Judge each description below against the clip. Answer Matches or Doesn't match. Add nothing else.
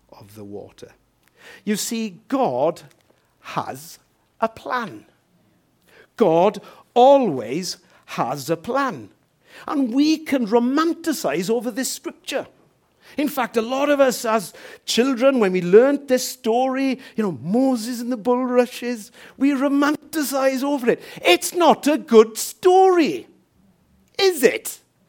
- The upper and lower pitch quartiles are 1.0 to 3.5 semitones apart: Doesn't match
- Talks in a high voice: Matches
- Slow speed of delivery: Matches